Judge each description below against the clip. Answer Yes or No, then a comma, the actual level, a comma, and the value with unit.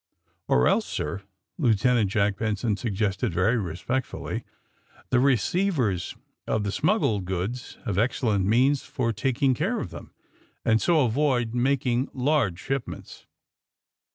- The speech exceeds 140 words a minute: No, slow, 135 wpm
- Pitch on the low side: Yes, low, 120 Hz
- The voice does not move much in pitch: No, average, 4.9 semitones